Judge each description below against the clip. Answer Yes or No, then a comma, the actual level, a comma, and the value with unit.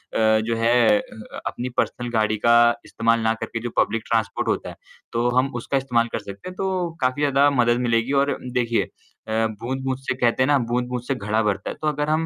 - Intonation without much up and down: No, average, 3.1 semitones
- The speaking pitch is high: No, low, 120 Hz